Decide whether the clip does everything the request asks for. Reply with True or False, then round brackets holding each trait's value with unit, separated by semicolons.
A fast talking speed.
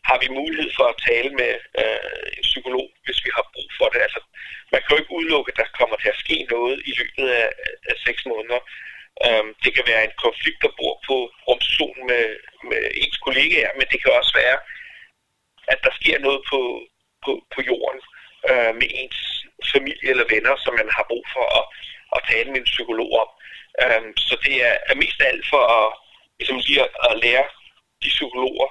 False (195 wpm)